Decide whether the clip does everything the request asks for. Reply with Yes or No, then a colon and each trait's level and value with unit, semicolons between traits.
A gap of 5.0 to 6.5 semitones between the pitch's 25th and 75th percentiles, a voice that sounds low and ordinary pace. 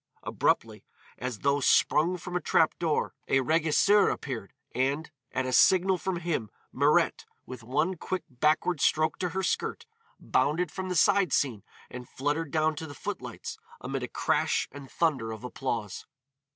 No: average, 5.3 semitones; medium, 155 Hz; average, 160 wpm